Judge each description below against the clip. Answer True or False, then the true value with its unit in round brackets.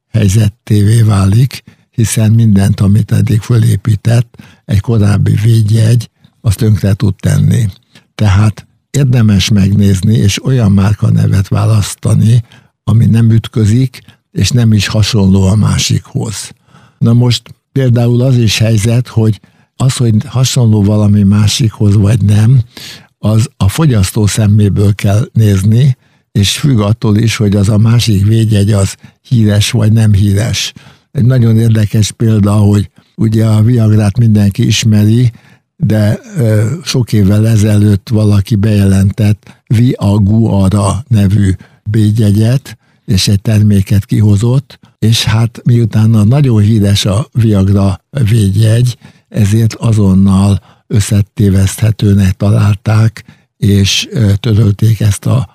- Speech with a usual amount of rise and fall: False (2.3 semitones)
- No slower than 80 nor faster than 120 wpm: True (110 wpm)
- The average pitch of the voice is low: True (110 Hz)